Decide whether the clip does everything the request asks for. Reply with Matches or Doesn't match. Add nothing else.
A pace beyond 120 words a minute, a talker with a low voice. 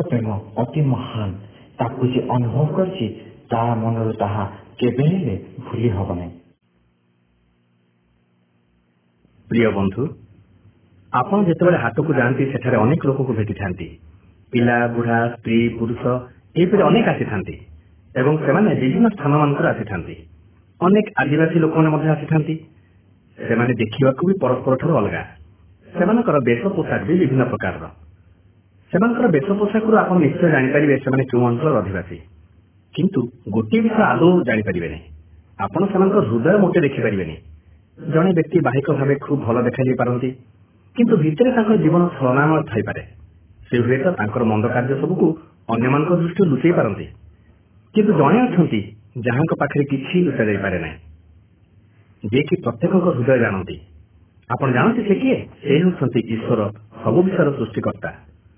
Doesn't match